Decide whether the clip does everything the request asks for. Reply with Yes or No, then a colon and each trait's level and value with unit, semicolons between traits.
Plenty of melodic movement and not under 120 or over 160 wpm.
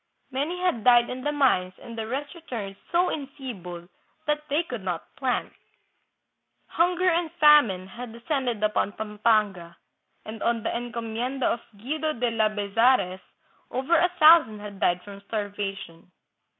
Yes: wide, 6.0 semitones; average, 145 wpm